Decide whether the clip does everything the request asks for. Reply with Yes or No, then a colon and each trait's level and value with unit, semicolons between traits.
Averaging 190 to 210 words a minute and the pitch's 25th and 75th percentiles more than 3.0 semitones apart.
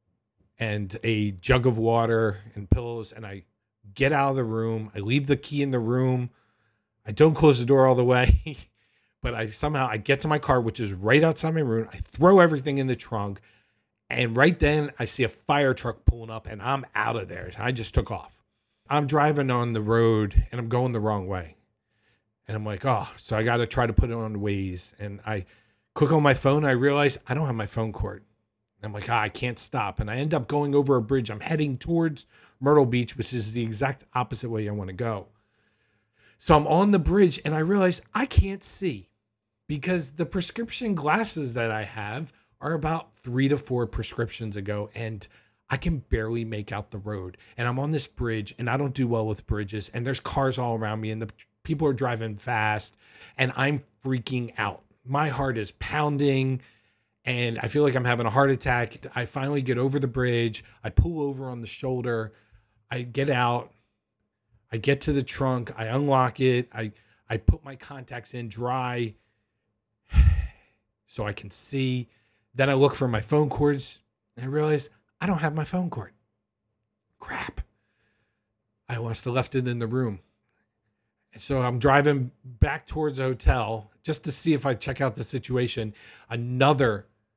Yes: average, 195 wpm; average, 4.1 semitones